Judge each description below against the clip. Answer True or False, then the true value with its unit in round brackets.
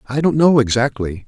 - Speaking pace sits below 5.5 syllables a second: True (5.2 syllables/s)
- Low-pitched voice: True (125 Hz)